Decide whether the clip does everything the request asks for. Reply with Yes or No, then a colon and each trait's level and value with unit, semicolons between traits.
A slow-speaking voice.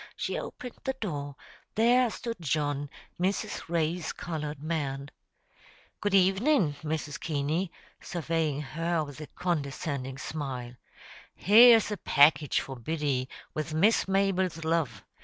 Yes: slow, 120 wpm